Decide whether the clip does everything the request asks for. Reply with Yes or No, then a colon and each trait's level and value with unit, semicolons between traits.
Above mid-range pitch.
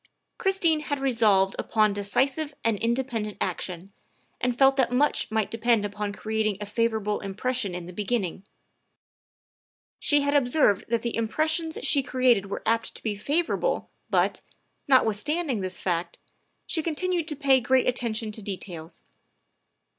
Yes: high, 230 Hz